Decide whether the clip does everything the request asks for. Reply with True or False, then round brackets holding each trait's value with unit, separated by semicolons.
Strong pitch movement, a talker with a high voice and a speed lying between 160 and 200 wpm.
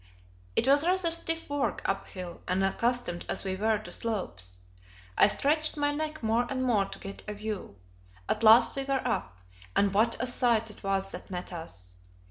True (5.8 semitones; 220 Hz; 180 wpm)